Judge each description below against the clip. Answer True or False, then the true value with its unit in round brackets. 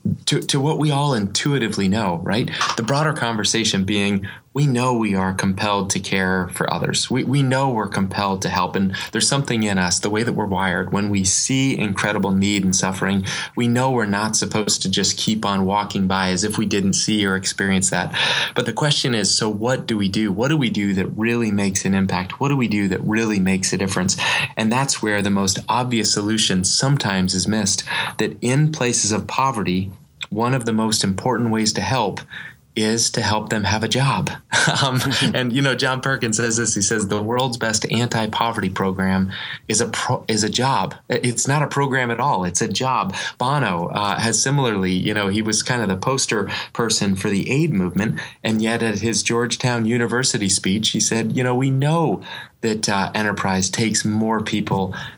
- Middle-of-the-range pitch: False (110 Hz)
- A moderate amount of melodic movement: True (4.0 semitones)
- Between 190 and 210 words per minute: True (205 wpm)